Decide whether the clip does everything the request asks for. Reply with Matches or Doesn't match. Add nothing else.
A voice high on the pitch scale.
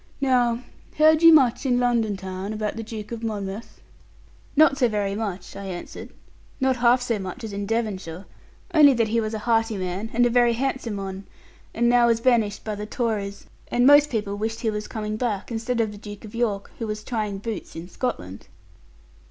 Matches